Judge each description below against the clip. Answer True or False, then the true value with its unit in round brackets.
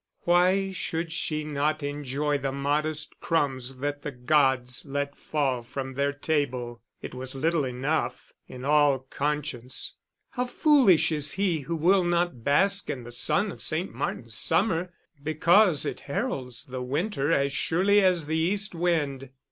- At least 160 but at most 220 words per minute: False (150 wpm)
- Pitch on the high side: False (150 Hz)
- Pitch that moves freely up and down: False (4.1 semitones)